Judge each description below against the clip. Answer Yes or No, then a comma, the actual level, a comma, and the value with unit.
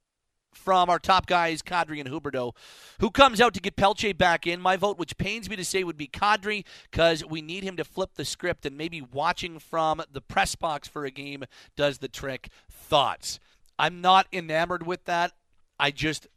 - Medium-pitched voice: Yes, medium, 170 Hz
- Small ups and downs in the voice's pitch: No, average, 4.3 semitones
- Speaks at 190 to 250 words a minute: Yes, average, 200 wpm